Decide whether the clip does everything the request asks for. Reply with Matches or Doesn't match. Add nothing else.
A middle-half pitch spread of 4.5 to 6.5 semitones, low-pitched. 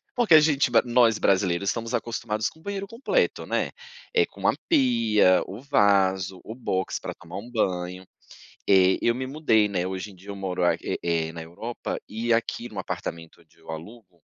Matches